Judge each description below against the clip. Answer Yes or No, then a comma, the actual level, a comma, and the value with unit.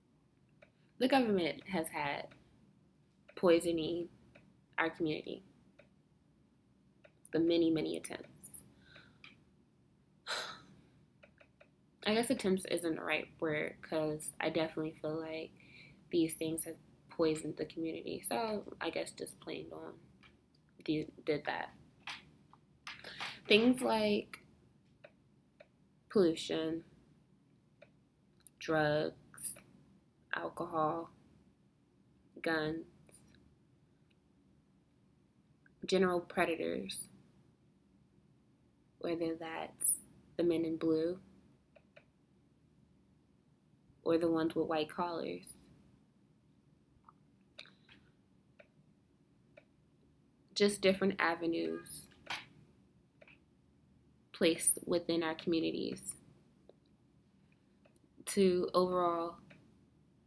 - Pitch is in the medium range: Yes, medium, 165 Hz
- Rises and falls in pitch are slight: Yes, narrow, 2.1 semitones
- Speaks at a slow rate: Yes, slow, 65 wpm